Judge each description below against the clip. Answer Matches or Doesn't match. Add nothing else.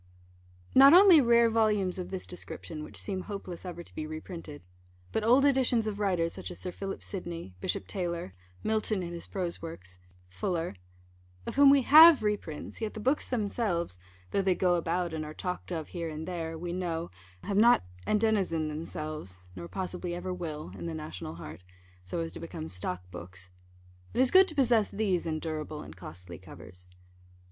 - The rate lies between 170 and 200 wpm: Matches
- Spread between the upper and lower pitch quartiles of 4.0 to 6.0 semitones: Matches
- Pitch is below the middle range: Doesn't match